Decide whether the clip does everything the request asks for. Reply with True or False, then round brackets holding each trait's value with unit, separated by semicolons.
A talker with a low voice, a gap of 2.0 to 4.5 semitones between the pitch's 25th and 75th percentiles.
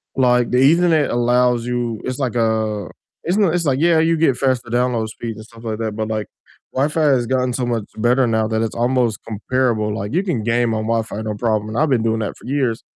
True (120 Hz; 2.9 semitones)